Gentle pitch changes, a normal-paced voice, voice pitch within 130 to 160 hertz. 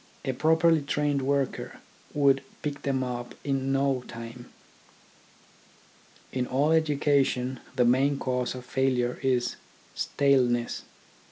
No: narrow, 2.2 semitones; slow, 110 wpm; low, 135 Hz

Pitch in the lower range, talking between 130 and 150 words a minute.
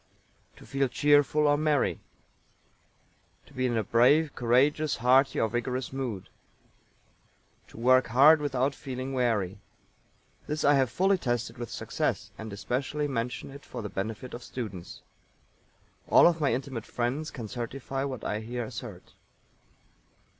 Yes: low, 130 Hz; average, 140 wpm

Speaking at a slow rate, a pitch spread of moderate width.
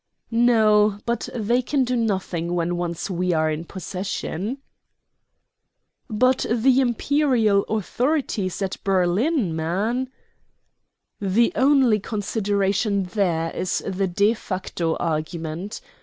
Yes: slow, 105 wpm; average, 4.8 semitones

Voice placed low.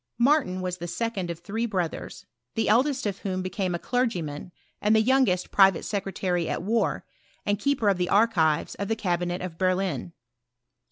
No: high, 190 Hz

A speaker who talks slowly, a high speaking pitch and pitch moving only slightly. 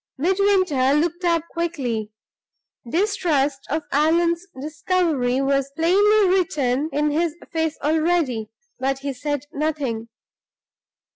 No: slow, 100 wpm; very high, 310 Hz; average, 4.0 semitones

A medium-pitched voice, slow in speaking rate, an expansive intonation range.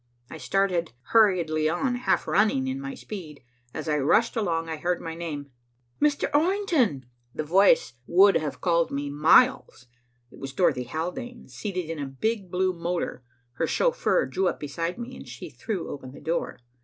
No: medium, 175 Hz; average, 170 wpm; wide, 6.5 semitones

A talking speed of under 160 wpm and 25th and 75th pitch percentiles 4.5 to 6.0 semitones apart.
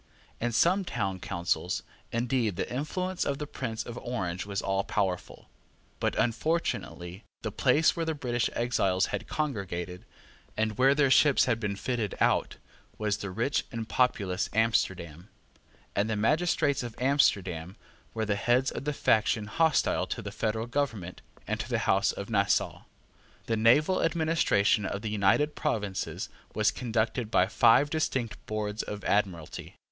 Yes: average, 150 wpm; average, 5.1 semitones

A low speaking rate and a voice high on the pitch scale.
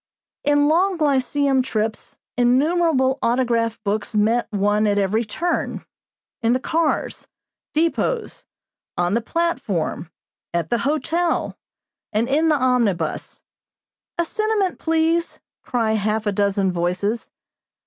Yes: slow, 115 wpm; high, 245 Hz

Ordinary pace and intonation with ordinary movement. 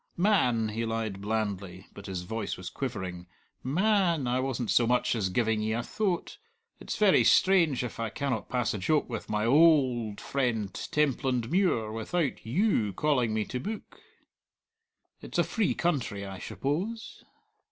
No: average, 165 wpm; wide, 6.2 semitones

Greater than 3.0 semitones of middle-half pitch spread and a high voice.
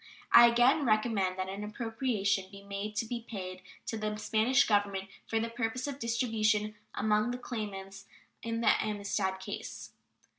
No: average, 2.7 semitones; high, 215 Hz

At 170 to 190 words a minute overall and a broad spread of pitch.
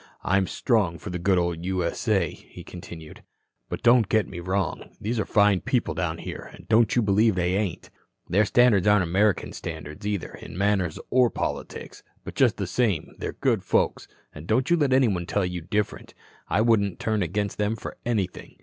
No: average, 185 wpm; average, 3.7 semitones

